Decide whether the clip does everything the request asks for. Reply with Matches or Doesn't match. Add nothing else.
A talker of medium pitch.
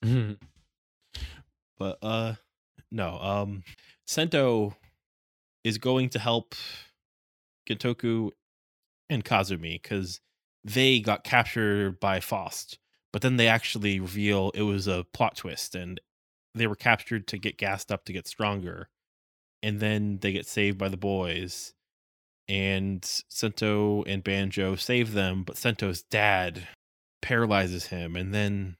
Doesn't match